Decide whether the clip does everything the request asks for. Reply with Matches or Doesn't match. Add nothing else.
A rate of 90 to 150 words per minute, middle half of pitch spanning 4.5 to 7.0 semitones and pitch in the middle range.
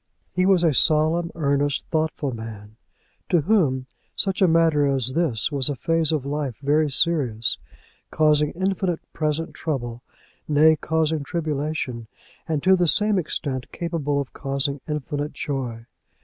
Doesn't match